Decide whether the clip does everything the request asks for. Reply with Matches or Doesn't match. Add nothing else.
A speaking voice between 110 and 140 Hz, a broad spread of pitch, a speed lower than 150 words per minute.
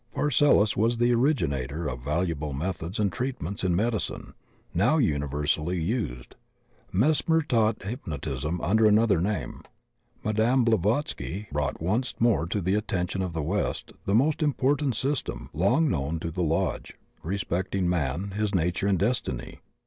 Doesn't match